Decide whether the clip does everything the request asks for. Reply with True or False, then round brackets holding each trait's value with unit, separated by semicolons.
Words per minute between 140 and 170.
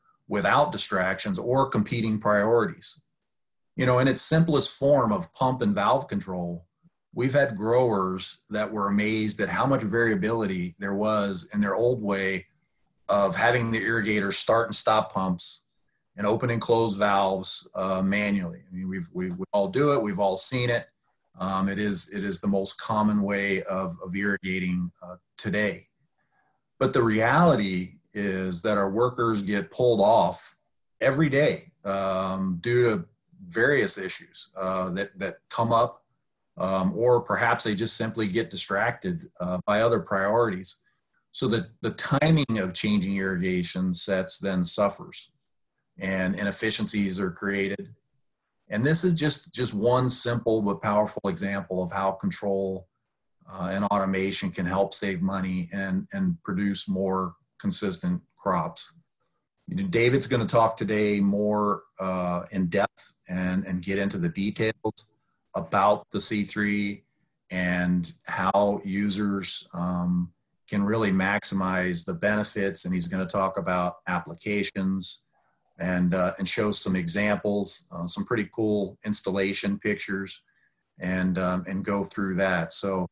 True (145 wpm)